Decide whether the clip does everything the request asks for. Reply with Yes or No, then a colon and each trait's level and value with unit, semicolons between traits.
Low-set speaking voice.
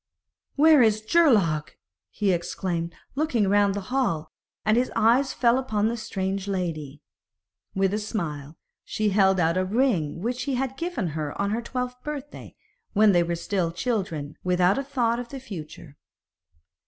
No: high, 205 Hz